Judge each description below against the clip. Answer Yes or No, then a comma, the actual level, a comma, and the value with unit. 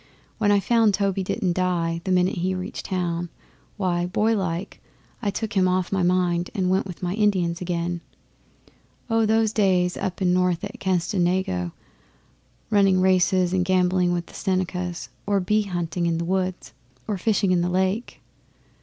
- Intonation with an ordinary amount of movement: No, narrow, 1.8 semitones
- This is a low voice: No, medium, 185 Hz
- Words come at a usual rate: Yes, average, 160 wpm